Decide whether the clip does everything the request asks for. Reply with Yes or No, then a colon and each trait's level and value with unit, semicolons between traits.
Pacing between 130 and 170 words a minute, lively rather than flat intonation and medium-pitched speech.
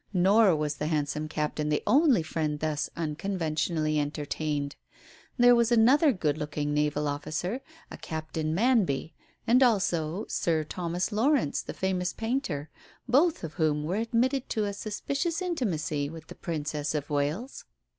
Yes: average, 145 wpm; wide, 7.1 semitones; medium, 165 Hz